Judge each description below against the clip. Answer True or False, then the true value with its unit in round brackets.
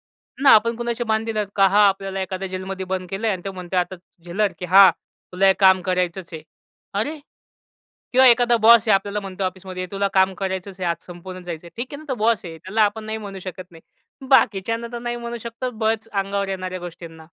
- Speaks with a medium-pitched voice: False (195 Hz)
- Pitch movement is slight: False (3.2 semitones)